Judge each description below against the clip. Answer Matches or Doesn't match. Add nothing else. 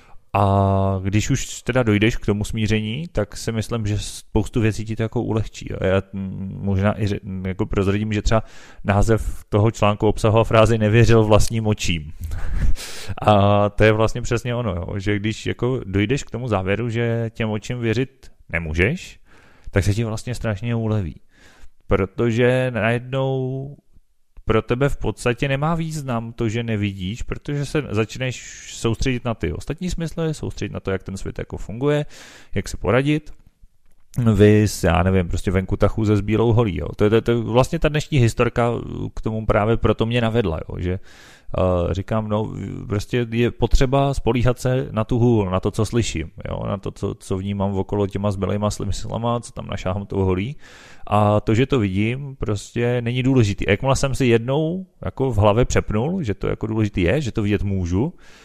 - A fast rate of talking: Matches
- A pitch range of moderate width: Matches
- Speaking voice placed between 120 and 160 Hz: Doesn't match